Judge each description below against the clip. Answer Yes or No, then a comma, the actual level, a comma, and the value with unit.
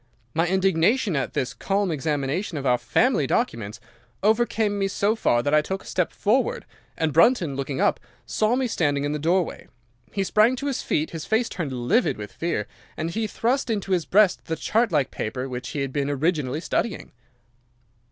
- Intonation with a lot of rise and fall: Yes, wide, 7.2 semitones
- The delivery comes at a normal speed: Yes, average, 190 wpm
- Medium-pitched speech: Yes, medium, 170 Hz